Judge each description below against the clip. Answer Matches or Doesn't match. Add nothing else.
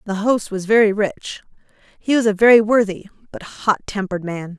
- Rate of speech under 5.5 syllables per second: Doesn't match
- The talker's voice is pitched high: Matches